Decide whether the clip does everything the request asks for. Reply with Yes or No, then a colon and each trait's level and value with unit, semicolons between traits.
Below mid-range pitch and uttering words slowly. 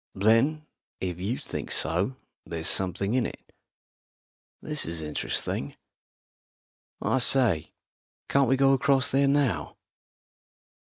Yes: low, 120 Hz; slow, 110 wpm